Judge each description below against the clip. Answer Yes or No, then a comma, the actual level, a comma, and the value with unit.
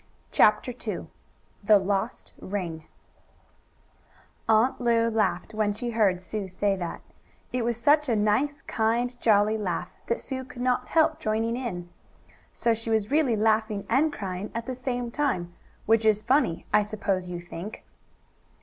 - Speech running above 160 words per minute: No, average, 155 wpm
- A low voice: No, high, 220 Hz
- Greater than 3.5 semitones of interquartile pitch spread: No, average, 3.2 semitones